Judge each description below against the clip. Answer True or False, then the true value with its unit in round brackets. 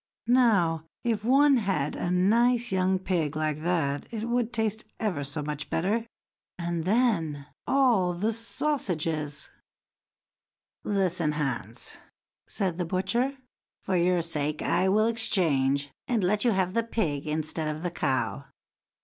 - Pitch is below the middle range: False (180 Hz)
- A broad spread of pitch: True (6.5 semitones)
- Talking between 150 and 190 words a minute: False (140 wpm)